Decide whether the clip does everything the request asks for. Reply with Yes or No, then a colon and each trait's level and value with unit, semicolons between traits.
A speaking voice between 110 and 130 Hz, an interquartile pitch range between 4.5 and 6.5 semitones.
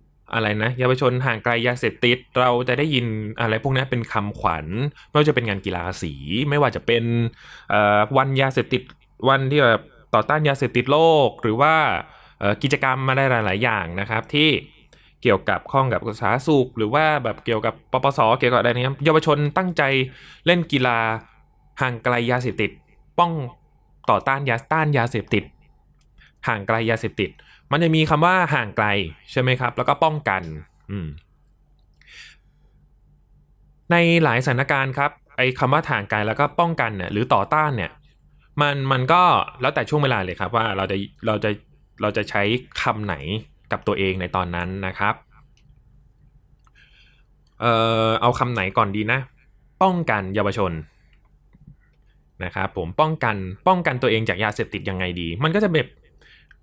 Yes: low, 120 Hz; average, 5.1 semitones